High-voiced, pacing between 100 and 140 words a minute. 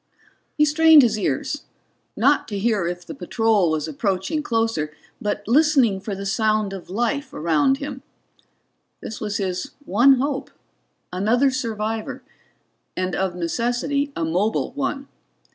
Yes: high, 220 Hz; slow, 135 wpm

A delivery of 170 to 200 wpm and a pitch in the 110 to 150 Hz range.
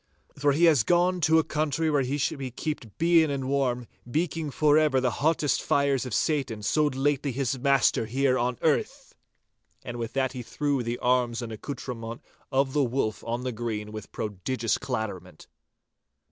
Yes: average, 175 wpm; low, 135 Hz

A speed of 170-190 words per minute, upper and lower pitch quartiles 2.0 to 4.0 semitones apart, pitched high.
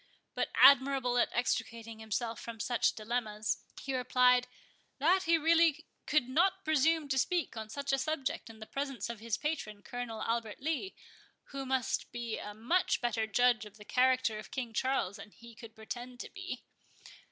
Yes: average, 175 wpm; average, 3.7 semitones; high, 245 Hz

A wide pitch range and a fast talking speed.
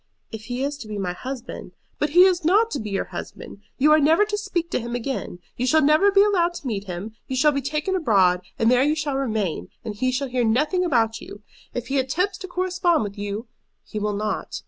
Yes: wide, 7.5 semitones; fast, 245 wpm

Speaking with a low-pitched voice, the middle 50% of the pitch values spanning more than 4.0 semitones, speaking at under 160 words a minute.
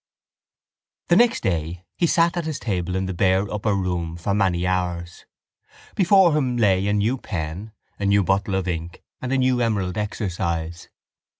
No: very low, 95 Hz; average, 5.1 semitones; average, 170 wpm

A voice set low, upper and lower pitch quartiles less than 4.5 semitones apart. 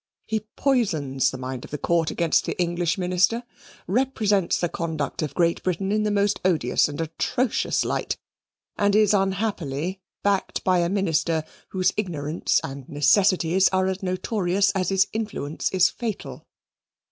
No: medium, 185 Hz; average, 3.8 semitones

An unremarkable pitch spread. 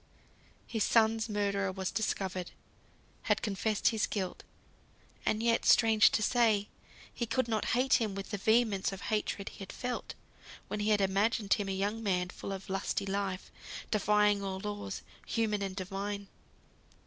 No: narrow, 2.1 semitones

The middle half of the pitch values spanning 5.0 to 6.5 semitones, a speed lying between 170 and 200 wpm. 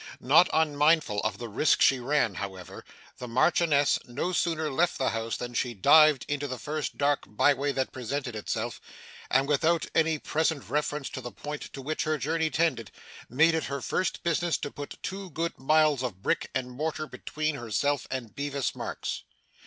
No: average, 3.8 semitones; average, 180 wpm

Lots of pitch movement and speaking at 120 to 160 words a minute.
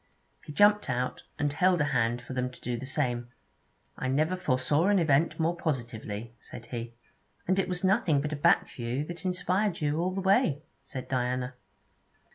No: wide, 6.1 semitones; average, 185 wpm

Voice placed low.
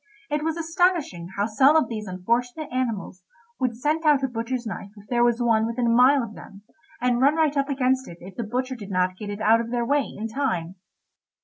No: high, 240 Hz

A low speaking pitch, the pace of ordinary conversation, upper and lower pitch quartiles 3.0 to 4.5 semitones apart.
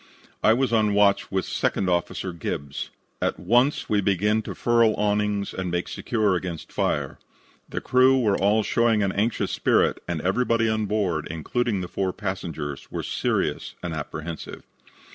Yes: low, 100 Hz; average, 160 wpm; average, 3.7 semitones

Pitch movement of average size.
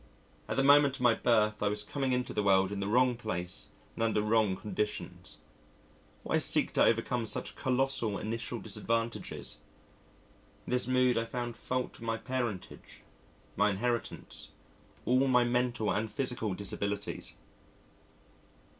Yes: average, 3.1 semitones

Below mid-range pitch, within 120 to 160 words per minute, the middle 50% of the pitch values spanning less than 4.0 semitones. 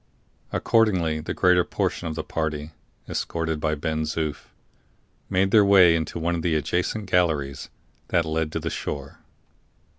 Yes: very low, 80 Hz; average, 150 wpm; narrow, 2.5 semitones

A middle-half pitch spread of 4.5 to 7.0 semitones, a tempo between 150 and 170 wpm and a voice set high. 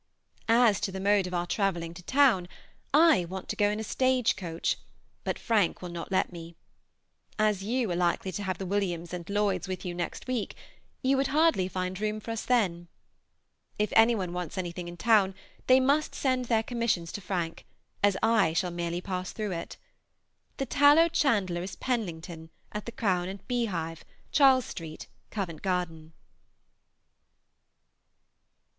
Yes: average, 4.8 semitones; average, 165 wpm; high, 195 Hz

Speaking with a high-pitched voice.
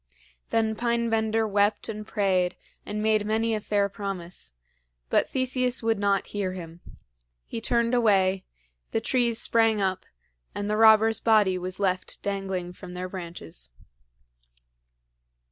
Yes: high, 210 Hz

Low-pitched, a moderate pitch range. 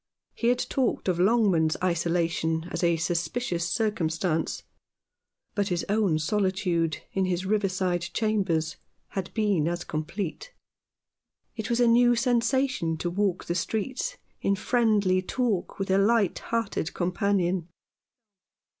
No: high, 190 Hz; average, 4.3 semitones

